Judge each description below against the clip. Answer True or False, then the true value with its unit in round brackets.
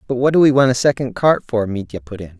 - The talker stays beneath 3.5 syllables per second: False (6.4 syllables/s)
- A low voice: True (120 Hz)